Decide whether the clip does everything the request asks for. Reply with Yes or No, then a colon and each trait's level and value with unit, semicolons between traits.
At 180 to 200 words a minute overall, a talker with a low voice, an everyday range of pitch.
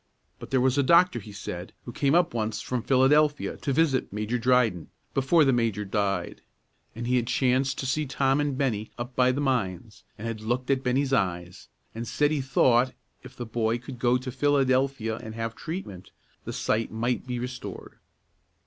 Yes: average, 190 wpm; low, 125 Hz; average, 3.3 semitones